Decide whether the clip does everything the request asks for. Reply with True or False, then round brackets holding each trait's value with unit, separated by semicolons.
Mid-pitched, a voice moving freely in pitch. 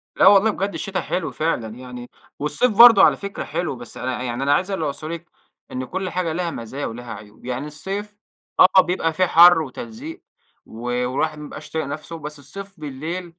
True (160 Hz; 5.9 semitones)